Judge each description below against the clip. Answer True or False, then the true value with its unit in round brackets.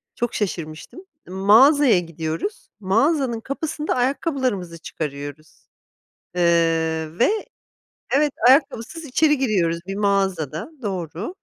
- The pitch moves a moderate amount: False (8.2 semitones)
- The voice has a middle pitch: False (200 Hz)